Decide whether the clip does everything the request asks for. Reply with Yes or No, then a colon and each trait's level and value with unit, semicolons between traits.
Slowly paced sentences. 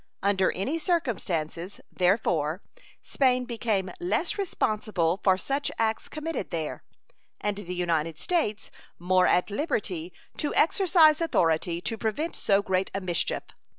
Yes: slow, 125 wpm